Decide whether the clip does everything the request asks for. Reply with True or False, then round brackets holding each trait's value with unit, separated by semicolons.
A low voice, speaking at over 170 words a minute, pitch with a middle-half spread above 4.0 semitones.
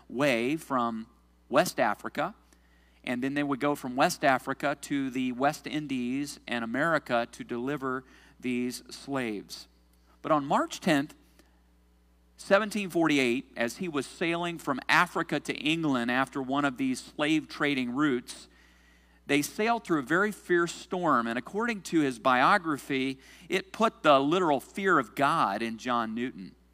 False (130 Hz; 145 wpm; 4.4 semitones)